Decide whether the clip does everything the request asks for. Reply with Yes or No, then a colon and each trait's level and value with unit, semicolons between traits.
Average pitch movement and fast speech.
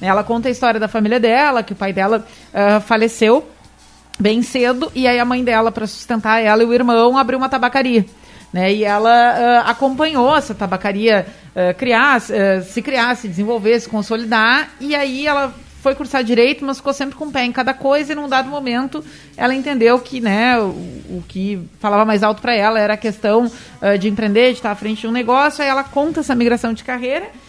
Yes: average, 3.5 semitones; fast, 210 wpm